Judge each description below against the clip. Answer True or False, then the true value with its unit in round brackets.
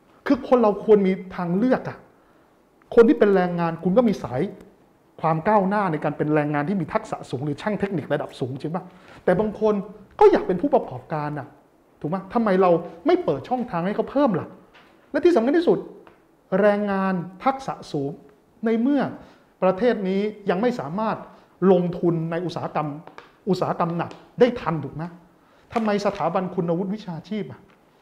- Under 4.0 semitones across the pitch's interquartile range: False (4.6 semitones)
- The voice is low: False (190 Hz)